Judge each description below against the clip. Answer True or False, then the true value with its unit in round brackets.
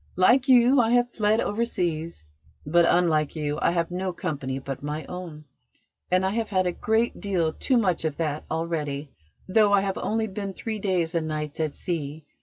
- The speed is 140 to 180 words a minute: False (190 wpm)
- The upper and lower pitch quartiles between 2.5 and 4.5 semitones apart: False (5.0 semitones)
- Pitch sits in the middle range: True (180 Hz)